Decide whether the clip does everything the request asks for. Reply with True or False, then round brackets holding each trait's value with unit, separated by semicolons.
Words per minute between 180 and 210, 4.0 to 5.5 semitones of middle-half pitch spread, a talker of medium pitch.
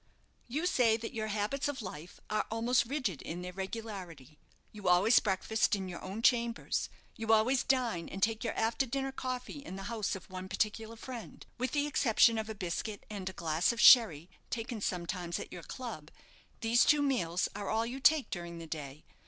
False (195 wpm; 4.6 semitones; 220 Hz)